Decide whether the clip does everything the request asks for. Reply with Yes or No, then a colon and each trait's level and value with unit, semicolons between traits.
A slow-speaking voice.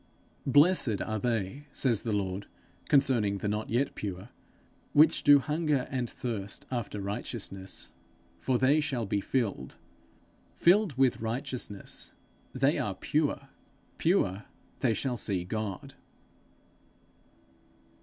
Yes: slow, 115 wpm